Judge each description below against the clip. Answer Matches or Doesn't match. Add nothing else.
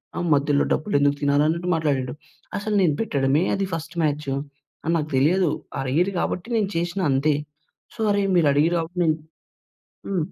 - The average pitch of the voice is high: Doesn't match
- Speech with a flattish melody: Doesn't match